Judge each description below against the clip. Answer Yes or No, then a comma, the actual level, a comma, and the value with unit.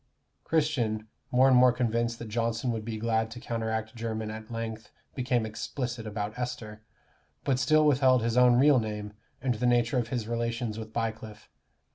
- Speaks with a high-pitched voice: No, low, 115 Hz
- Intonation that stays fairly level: Yes, narrow, 2.0 semitones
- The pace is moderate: Yes, average, 170 wpm